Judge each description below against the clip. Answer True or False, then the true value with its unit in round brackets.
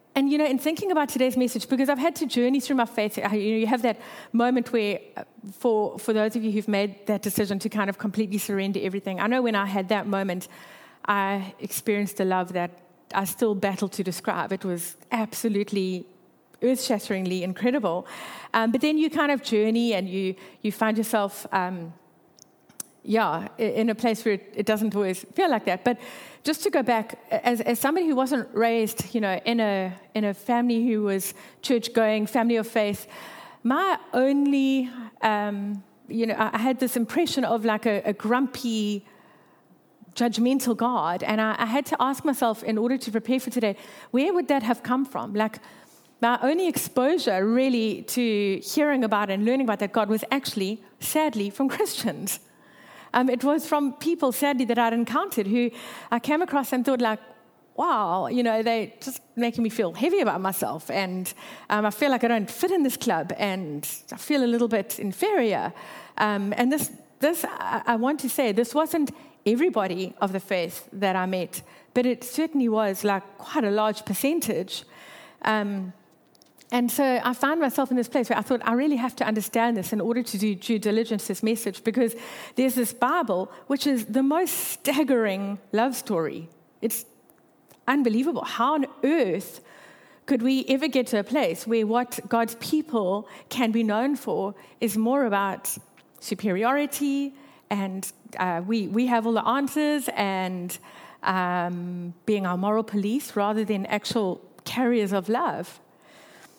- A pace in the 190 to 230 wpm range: False (175 wpm)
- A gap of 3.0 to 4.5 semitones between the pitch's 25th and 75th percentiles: True (4.2 semitones)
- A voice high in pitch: True (230 Hz)